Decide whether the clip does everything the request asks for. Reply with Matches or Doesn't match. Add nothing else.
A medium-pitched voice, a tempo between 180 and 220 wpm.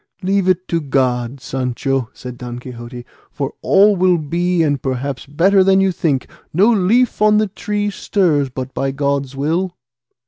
Doesn't match